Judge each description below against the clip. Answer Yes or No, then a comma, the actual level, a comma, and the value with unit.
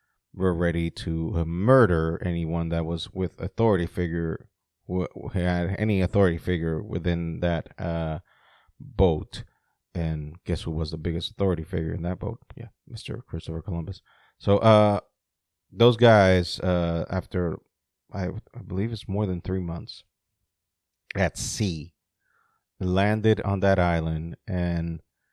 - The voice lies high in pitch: No, very low, 90 Hz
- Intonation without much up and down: No, average, 3.2 semitones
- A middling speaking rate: No, slow, 130 wpm